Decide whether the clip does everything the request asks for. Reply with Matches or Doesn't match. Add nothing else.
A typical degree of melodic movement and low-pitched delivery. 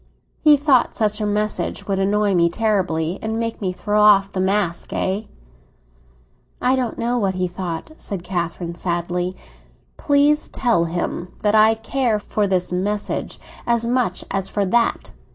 Doesn't match